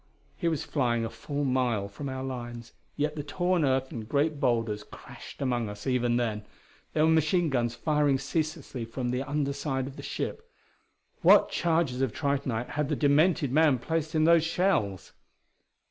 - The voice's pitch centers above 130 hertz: Yes, medium, 140 Hz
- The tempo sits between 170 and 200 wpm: Yes, average, 175 wpm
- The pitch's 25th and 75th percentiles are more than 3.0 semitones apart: Yes, average, 4.3 semitones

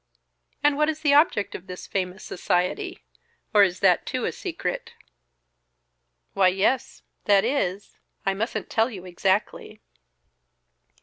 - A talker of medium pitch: No, high, 200 Hz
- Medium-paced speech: No, slow, 130 wpm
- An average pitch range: No, wide, 6.9 semitones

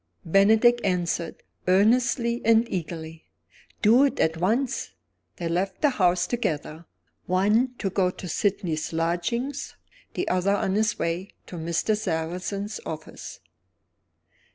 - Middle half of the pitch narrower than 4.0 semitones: No, average, 4.7 semitones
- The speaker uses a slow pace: Yes, slow, 120 wpm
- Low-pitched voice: No, high, 190 Hz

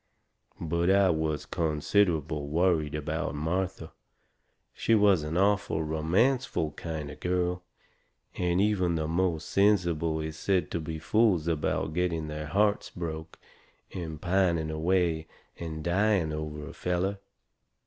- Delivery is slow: Yes, slow, 130 wpm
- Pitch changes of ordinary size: Yes, average, 3.1 semitones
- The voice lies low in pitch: Yes, very low, 85 Hz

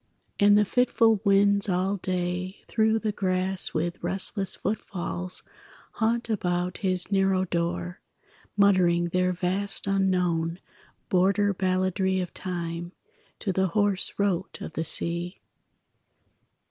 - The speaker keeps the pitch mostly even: Yes, narrow, 2.1 semitones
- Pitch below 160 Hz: No, medium, 185 Hz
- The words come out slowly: Yes, slow, 115 wpm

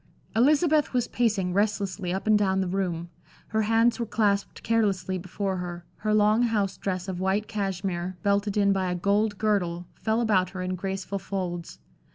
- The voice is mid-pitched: No, high, 195 Hz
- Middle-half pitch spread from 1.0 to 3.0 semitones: Yes, narrow, 2.6 semitones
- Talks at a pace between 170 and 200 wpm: Yes, average, 175 wpm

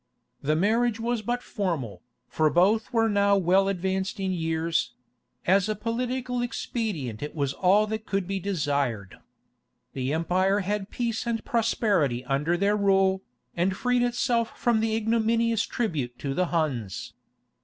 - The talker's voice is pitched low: No, high, 195 Hz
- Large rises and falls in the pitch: Yes, wide, 5.7 semitones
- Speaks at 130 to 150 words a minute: Yes, average, 145 wpm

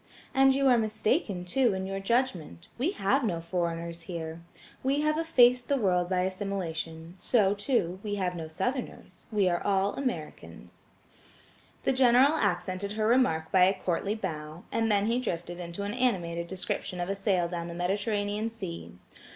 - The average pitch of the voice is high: Yes, high, 195 Hz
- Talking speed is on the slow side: No, average, 160 wpm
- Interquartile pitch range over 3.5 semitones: Yes, average, 5.3 semitones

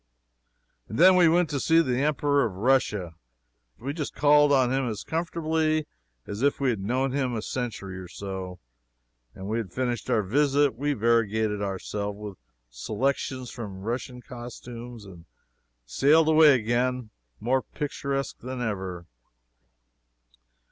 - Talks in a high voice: No, low, 125 Hz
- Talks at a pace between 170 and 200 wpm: No, average, 145 wpm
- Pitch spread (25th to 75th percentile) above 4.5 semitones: Yes, average, 5.3 semitones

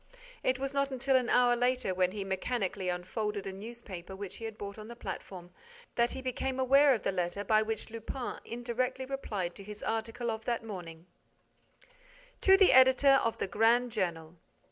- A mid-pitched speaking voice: No, high, 225 Hz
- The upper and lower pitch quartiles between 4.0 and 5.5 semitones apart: Yes, average, 4.7 semitones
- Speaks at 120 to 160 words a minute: No, average, 185 wpm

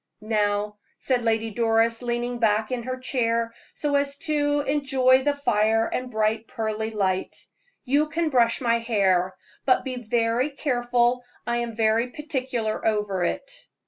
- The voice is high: Yes, high, 235 Hz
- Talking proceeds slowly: No, average, 145 wpm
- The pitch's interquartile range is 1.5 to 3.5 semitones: Yes, average, 2.9 semitones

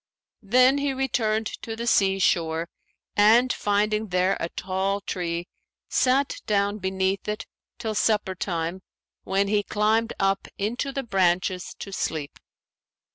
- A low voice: No, high, 200 Hz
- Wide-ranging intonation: No, average, 2.9 semitones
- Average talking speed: No, slow, 130 wpm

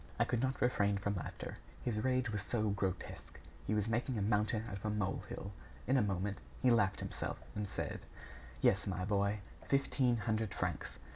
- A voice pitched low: Yes, low, 105 Hz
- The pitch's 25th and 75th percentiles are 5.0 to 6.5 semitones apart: No, average, 3.0 semitones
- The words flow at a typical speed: Yes, average, 185 wpm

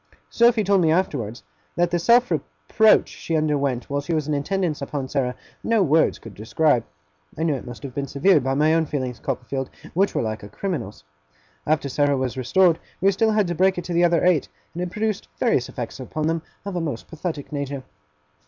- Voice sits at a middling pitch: Yes, medium, 155 Hz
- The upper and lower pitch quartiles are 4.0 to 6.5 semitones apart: Yes, average, 5.0 semitones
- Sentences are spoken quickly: Yes, fast, 210 wpm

